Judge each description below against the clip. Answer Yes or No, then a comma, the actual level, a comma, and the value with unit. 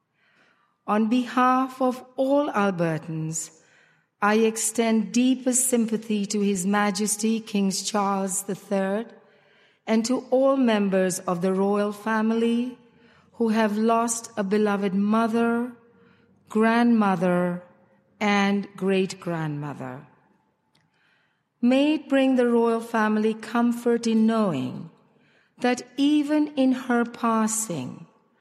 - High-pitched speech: Yes, high, 220 Hz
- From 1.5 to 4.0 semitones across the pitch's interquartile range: Yes, average, 3.0 semitones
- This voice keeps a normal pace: No, slow, 100 wpm